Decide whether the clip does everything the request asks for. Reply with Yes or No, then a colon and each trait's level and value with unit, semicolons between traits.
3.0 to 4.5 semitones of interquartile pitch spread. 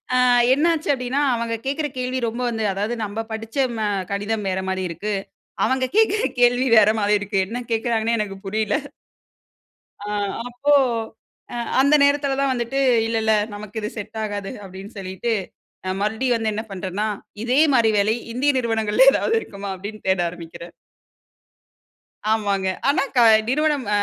Yes: average, 3.9 semitones